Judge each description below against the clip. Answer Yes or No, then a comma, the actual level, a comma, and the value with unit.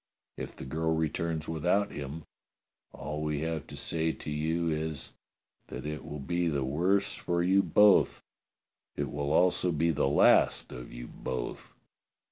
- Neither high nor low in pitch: No, very low, 80 Hz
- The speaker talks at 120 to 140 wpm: No, average, 155 wpm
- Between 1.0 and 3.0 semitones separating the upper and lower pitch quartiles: Yes, narrow, 2.5 semitones